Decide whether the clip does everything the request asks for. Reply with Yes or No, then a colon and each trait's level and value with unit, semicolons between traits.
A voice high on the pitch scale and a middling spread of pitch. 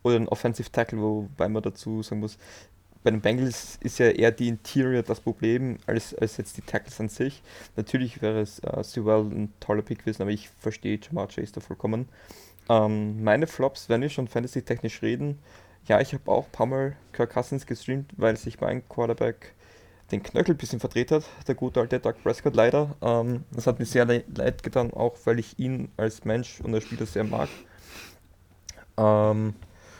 No: low, 115 Hz; average, 3.0 semitones